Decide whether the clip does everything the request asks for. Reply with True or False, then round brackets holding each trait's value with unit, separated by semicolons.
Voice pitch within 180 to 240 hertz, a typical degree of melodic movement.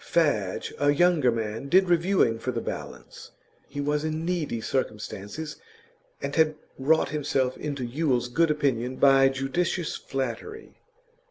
False (140 Hz; 4.1 semitones)